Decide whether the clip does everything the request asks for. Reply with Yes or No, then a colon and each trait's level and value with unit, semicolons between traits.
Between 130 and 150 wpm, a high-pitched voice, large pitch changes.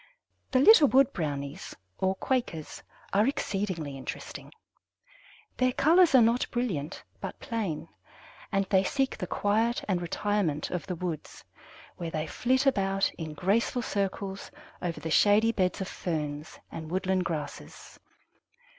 Yes: slow, 135 wpm; high, 195 Hz; wide, 6.1 semitones